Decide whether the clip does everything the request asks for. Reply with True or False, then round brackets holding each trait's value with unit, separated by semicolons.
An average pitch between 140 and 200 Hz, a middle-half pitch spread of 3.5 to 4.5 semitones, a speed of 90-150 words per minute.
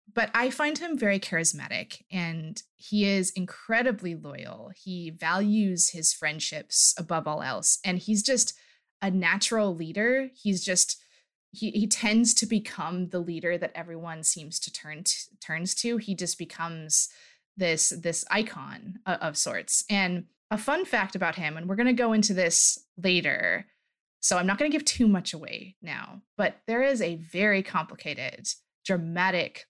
False (190 Hz; 4.1 semitones; 160 wpm)